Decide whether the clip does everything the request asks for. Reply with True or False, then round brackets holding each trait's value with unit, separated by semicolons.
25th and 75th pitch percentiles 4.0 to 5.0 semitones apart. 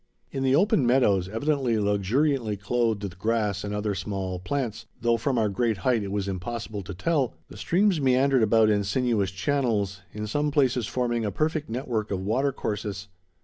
True (4.4 semitones)